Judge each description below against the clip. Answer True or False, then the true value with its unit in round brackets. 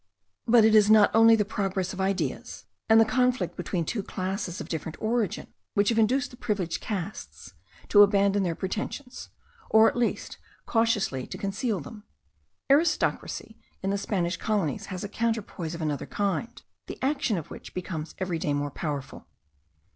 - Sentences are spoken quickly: False (165 wpm)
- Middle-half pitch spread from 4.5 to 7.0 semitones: False (3.7 semitones)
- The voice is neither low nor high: False (200 Hz)